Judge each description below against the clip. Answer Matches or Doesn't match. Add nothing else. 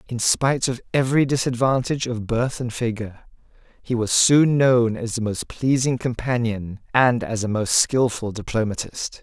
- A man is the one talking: Matches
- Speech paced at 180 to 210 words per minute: Doesn't match